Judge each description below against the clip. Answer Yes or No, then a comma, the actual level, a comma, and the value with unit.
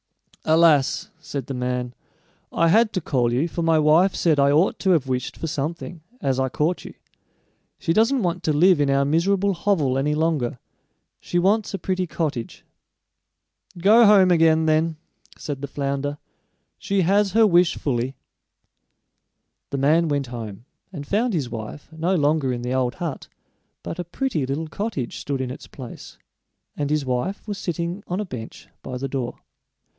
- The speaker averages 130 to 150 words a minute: No, average, 170 wpm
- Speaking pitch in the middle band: Yes, medium, 155 Hz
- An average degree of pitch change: Yes, average, 4.9 semitones